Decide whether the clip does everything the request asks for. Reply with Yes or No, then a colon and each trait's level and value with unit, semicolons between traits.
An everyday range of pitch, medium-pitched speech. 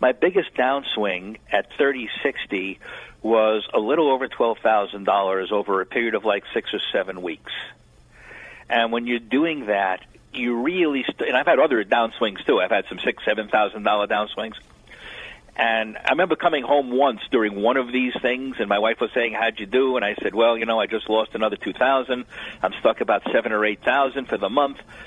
No: average, 3.3 semitones; low, 115 Hz